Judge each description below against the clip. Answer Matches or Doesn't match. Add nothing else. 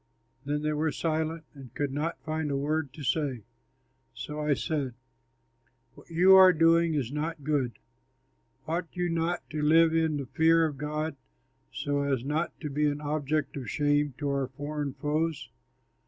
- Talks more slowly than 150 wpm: Doesn't match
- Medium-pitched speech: Matches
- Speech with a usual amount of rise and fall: Doesn't match